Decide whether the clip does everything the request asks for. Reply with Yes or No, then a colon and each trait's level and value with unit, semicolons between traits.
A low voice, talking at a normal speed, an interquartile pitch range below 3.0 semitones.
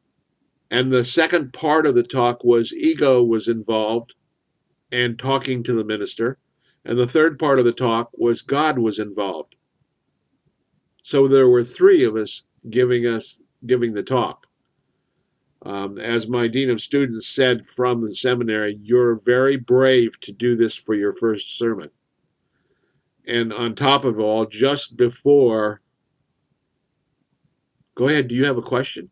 Yes: low, 120 Hz; average, 150 wpm; narrow, 2.4 semitones